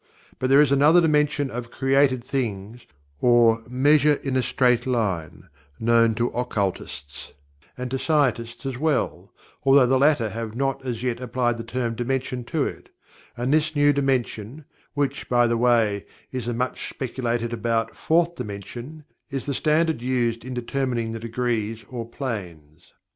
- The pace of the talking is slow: No, average, 155 wpm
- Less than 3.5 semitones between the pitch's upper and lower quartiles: Yes, average, 2.8 semitones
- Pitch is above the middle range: No, low, 125 Hz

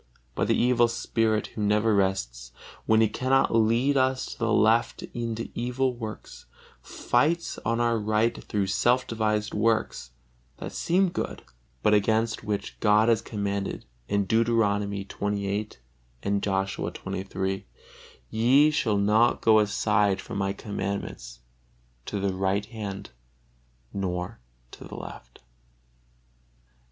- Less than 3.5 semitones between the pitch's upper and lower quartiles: Yes, narrow, 2.5 semitones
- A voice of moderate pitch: No, low, 105 Hz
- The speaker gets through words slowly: Yes, slow, 125 wpm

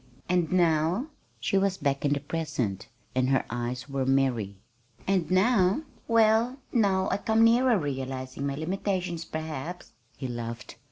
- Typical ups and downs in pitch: No, wide, 6.6 semitones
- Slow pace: No, average, 145 wpm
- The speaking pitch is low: No, medium, 160 Hz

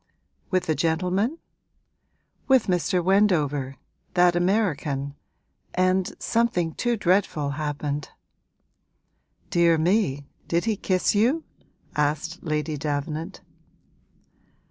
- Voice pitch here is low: No, medium, 175 Hz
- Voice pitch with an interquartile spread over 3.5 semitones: Yes, average, 4.4 semitones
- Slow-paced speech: Yes, slow, 90 wpm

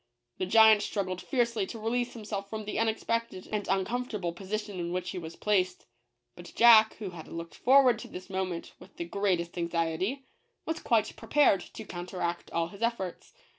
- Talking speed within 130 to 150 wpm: No, average, 170 wpm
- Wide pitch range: No, average, 4.0 semitones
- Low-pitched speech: No, high, 200 Hz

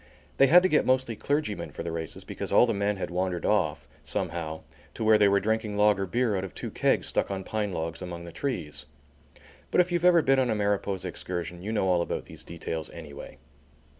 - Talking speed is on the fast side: Yes, fast, 220 wpm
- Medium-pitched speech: No, low, 100 Hz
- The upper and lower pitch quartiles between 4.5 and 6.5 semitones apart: Yes, average, 5.0 semitones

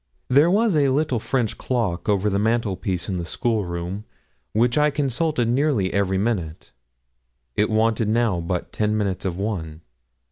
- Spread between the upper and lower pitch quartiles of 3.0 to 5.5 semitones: Yes, average, 4.8 semitones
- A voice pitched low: Yes, low, 110 Hz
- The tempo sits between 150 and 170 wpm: Yes, average, 155 wpm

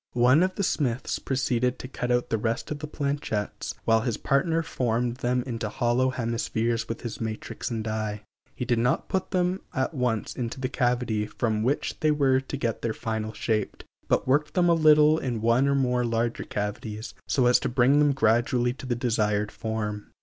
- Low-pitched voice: Yes, low, 120 Hz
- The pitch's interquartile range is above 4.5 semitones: No, average, 3.1 semitones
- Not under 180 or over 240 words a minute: Yes, average, 200 wpm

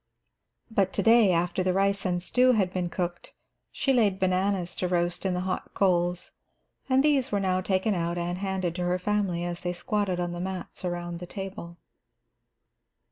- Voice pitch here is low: No, medium, 185 Hz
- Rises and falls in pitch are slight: Yes, narrow, 2.1 semitones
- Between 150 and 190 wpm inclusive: Yes, average, 185 wpm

